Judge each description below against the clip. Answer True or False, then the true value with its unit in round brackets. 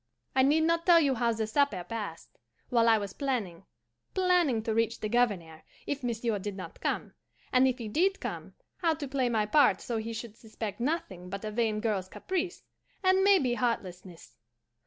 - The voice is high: True (230 Hz)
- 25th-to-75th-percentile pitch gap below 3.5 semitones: False (5.3 semitones)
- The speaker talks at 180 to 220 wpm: True (185 wpm)